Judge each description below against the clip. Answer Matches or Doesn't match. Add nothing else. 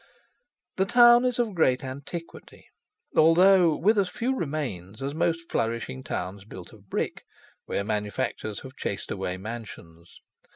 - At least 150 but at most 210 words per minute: Doesn't match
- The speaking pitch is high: Doesn't match